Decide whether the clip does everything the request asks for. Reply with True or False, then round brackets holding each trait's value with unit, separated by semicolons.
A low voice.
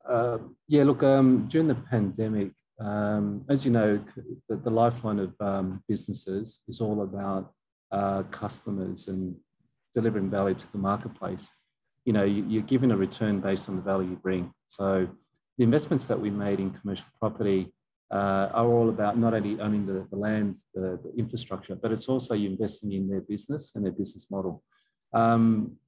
True (105 Hz)